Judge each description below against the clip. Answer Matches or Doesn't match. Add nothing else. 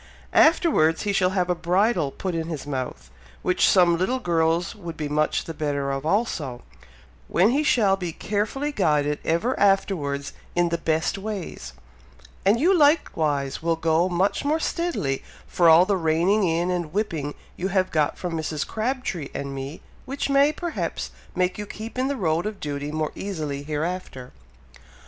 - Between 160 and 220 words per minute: Matches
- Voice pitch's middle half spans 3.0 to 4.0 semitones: Doesn't match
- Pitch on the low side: Doesn't match